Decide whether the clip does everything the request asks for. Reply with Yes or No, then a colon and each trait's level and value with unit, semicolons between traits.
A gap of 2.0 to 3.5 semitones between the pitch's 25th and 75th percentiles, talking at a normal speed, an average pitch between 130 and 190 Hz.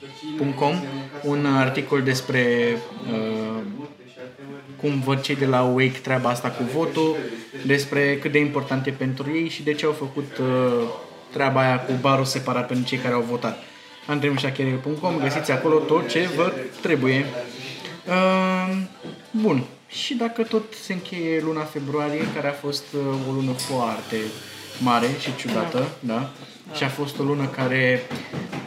Yes: average, 2.8 semitones; average, 150 wpm; medium, 140 Hz